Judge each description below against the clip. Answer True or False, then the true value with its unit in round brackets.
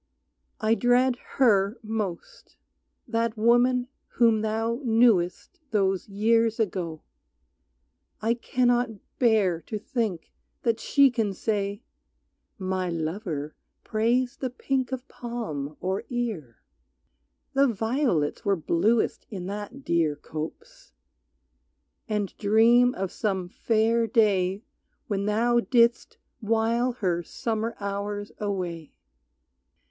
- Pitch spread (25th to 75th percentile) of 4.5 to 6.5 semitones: False (3.8 semitones)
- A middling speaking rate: False (105 wpm)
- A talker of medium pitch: False (220 Hz)